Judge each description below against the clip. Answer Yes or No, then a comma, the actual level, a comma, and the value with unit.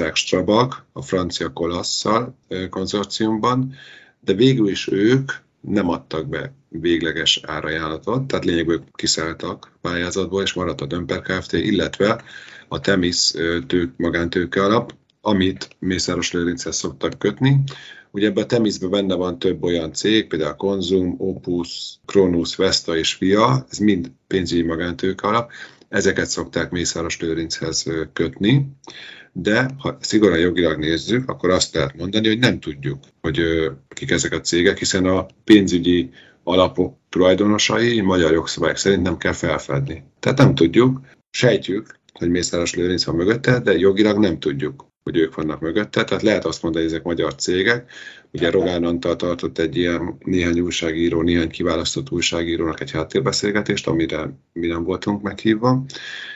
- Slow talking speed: No, average, 140 wpm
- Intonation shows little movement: No, average, 3.7 semitones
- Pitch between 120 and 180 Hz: No, very low, 90 Hz